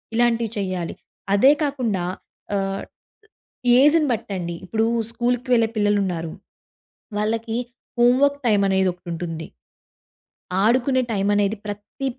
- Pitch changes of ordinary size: Yes, average, 3.8 semitones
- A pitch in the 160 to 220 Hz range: Yes, high, 210 Hz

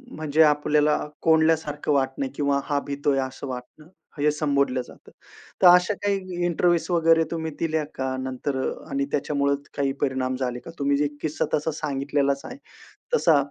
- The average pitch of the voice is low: No, medium, 145 Hz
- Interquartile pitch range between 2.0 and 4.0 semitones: Yes, narrow, 2.6 semitones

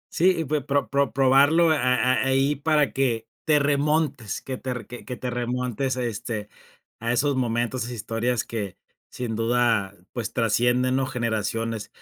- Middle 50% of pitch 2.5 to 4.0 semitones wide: Yes, average, 3.0 semitones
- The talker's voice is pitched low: Yes, low, 125 Hz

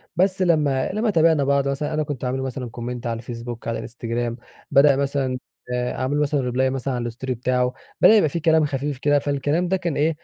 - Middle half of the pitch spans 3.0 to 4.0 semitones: Yes, average, 3.3 semitones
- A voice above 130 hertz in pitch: Yes, medium, 140 Hz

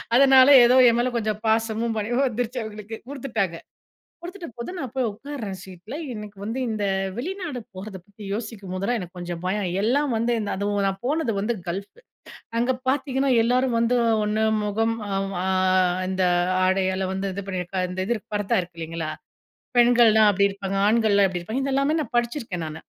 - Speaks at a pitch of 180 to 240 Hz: Yes, high, 220 Hz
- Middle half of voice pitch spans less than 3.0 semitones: No, average, 4.1 semitones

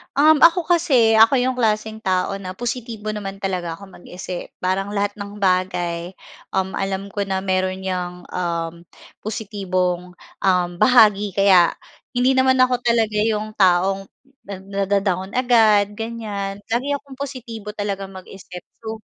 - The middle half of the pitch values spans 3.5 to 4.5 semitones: No, average, 3.0 semitones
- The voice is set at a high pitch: Yes, high, 200 Hz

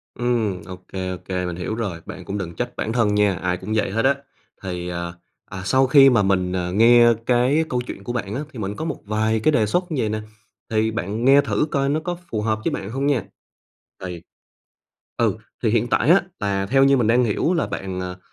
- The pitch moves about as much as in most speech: Yes, average, 4.7 semitones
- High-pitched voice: No, low, 110 Hz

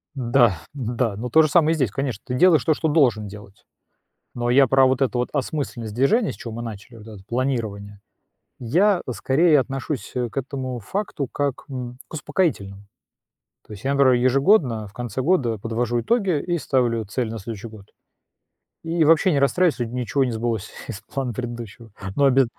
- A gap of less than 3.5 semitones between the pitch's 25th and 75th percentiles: No, average, 3.8 semitones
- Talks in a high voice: No, low, 125 Hz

